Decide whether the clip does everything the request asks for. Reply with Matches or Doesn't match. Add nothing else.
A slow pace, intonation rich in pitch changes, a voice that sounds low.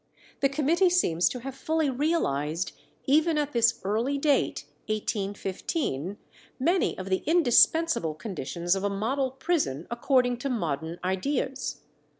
Doesn't match